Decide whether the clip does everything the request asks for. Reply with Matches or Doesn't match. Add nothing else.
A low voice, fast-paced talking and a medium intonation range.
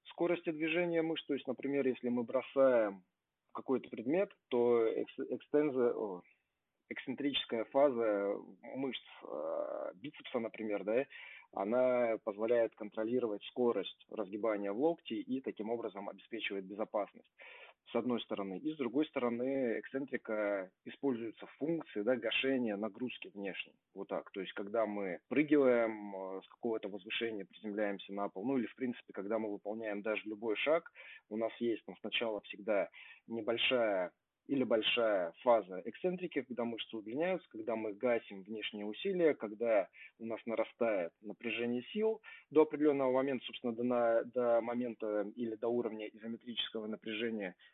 Doesn't match